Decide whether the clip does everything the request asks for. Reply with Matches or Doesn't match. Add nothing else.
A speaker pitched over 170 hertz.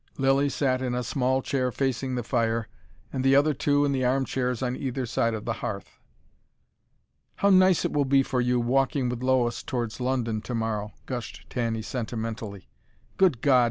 Doesn't match